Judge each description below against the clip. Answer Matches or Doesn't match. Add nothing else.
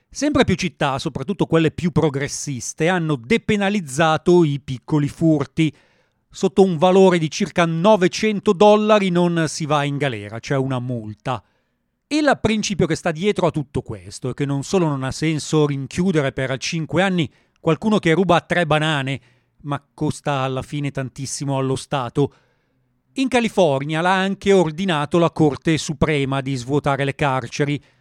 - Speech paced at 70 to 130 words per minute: Doesn't match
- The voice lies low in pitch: Doesn't match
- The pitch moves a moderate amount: Matches